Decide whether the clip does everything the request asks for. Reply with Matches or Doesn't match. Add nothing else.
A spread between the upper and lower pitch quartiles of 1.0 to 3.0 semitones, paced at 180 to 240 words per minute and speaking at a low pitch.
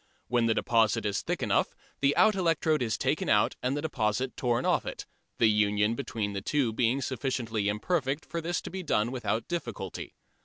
Doesn't match